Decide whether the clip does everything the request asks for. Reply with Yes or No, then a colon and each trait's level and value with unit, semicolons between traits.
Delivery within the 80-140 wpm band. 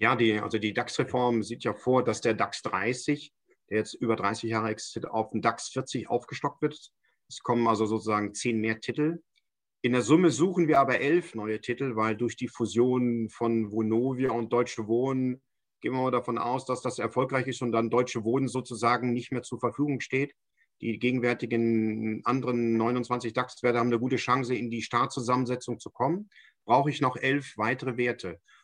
No: average, 185 wpm